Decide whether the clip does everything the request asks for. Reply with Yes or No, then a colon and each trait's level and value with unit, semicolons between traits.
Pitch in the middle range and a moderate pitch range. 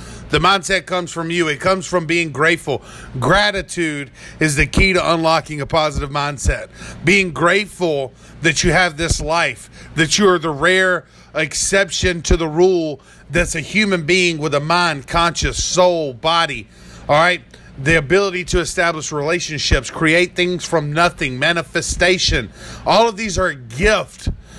Yes: medium, 170 Hz; average, 3.0 semitones